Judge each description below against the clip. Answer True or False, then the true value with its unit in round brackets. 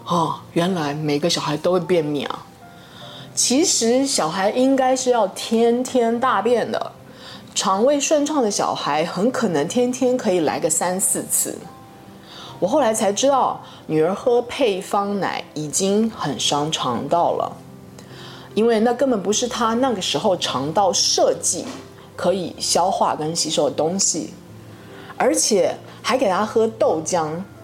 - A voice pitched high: True (215 Hz)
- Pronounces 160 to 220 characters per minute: True (210 characters per minute)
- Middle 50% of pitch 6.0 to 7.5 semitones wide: True (6.7 semitones)